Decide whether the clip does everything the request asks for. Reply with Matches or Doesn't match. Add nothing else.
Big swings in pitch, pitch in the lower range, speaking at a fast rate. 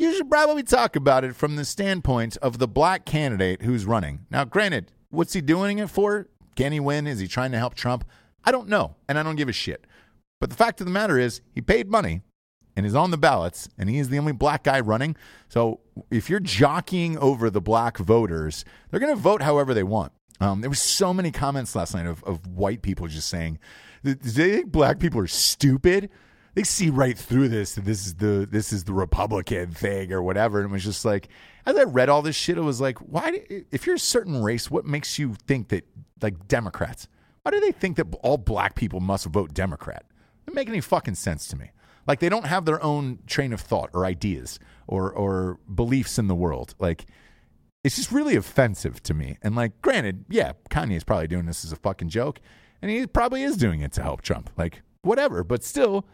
Matches